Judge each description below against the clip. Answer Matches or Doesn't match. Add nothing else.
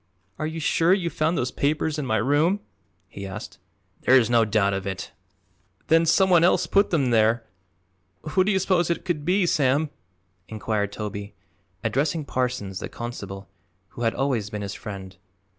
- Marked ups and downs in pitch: Matches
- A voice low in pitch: Matches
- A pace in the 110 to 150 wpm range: Doesn't match